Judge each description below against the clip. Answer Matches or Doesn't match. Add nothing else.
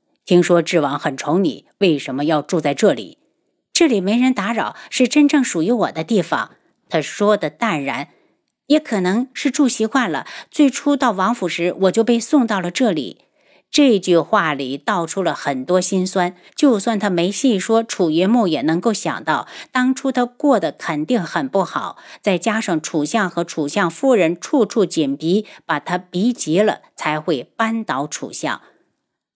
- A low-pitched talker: Doesn't match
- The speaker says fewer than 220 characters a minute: Doesn't match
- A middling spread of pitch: Doesn't match